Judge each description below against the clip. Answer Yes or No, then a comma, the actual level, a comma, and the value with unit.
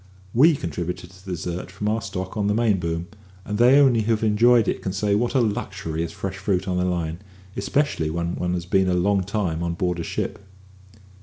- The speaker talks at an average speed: No, fast, 225 wpm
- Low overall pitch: Yes, very low, 95 Hz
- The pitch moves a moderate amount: Yes, average, 3.4 semitones